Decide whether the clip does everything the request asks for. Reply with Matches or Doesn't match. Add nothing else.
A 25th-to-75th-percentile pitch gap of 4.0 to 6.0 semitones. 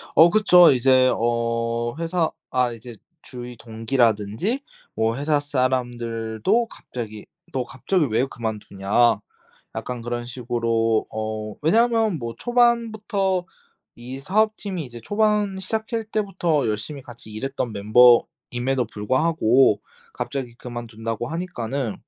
Doesn't match